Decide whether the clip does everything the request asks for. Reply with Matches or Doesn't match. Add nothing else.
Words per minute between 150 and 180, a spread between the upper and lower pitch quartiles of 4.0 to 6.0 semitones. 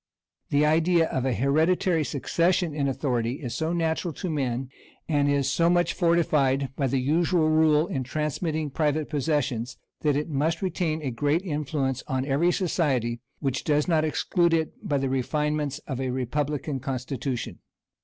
Doesn't match